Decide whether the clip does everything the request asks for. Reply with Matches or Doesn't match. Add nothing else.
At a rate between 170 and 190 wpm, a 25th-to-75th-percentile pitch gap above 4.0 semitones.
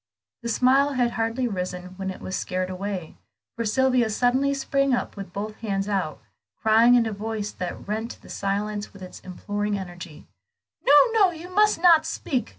Matches